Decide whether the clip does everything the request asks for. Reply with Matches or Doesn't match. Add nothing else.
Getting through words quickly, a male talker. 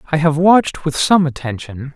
Doesn't match